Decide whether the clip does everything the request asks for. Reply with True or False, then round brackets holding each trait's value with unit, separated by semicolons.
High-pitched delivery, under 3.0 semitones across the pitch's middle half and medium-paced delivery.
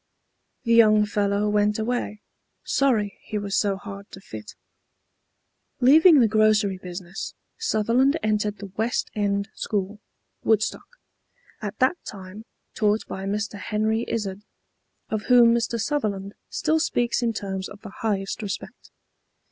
False (210 Hz; 2.4 semitones; 130 wpm)